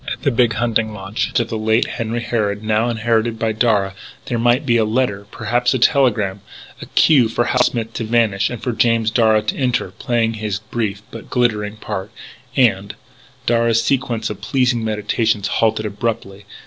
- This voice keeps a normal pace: Yes, average, 175 wpm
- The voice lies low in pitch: Yes, low, 115 Hz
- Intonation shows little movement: Yes, narrow, 2.0 semitones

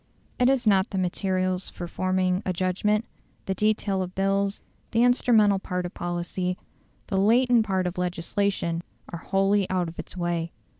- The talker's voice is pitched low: No, high, 190 Hz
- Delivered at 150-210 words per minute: Yes, average, 160 wpm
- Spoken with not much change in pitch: Yes, narrow, 2.2 semitones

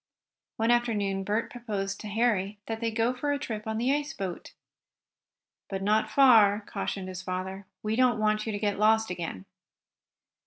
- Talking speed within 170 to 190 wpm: Yes, average, 180 wpm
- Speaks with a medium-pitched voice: No, high, 215 Hz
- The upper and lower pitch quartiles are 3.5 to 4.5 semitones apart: No, average, 2.8 semitones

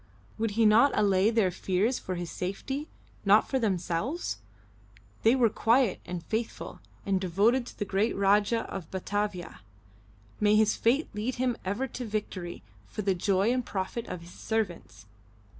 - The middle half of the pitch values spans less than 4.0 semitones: Yes, average, 3.6 semitones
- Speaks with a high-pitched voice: Yes, high, 210 Hz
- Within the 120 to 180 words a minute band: Yes, average, 160 wpm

